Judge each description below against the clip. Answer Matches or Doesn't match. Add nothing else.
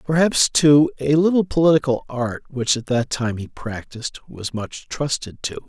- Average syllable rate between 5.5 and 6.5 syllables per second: Doesn't match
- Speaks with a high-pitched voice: Doesn't match